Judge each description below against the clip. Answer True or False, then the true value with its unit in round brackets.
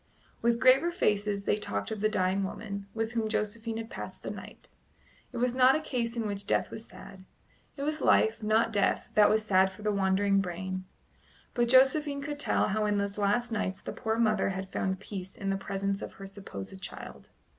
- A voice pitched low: False (210 Hz)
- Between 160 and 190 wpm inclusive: False (205 wpm)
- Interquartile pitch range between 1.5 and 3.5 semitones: True (2.9 semitones)